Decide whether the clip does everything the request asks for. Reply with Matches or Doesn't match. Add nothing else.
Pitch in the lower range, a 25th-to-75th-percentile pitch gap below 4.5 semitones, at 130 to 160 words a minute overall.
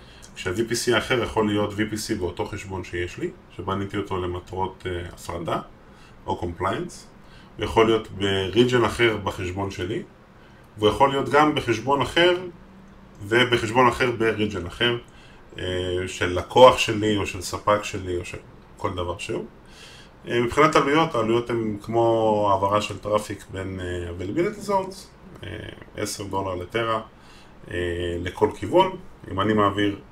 Matches